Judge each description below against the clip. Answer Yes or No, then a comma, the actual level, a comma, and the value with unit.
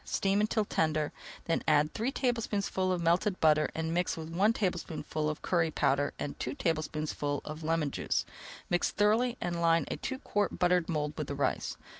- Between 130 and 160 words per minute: No, average, 180 wpm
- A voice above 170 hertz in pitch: No, medium, 165 Hz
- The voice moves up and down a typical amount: Yes, average, 4.3 semitones